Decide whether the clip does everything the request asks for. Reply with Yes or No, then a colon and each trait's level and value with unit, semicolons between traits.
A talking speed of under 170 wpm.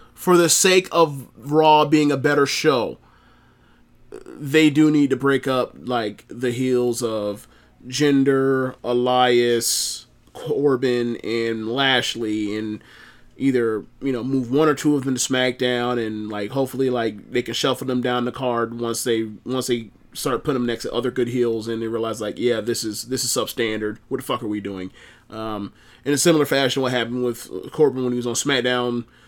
No: average, 180 wpm